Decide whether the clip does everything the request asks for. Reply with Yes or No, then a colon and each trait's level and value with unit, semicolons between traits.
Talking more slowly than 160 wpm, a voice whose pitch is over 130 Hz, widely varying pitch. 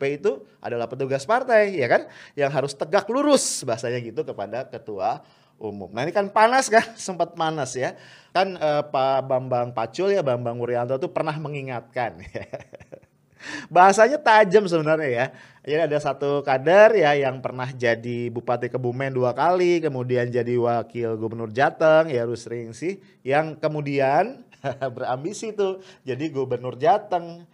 Yes: average, 145 wpm; medium, 140 Hz; wide, 6.8 semitones